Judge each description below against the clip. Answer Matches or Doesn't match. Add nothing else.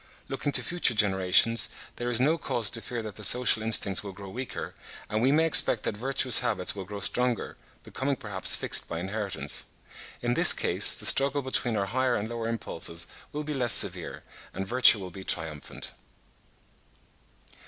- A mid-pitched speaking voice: Doesn't match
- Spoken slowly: Doesn't match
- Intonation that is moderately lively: Matches